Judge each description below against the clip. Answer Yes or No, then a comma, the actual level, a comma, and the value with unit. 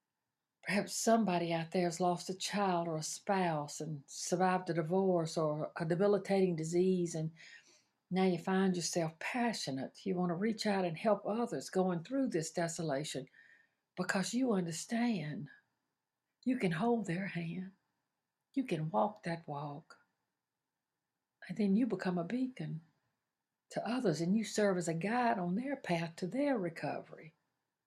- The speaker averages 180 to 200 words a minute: No, average, 150 wpm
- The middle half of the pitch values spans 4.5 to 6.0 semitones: No, average, 3.4 semitones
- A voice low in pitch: No, medium, 180 Hz